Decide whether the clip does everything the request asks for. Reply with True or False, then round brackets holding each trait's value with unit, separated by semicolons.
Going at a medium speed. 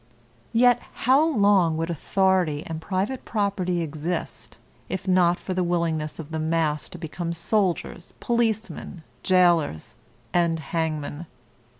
False (120 wpm)